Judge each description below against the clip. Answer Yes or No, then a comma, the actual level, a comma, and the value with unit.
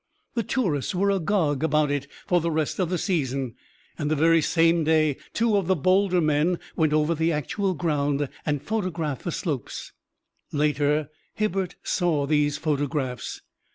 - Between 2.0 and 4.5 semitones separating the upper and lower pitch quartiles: Yes, average, 3.6 semitones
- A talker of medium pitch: Yes, medium, 155 Hz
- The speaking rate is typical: Yes, average, 155 wpm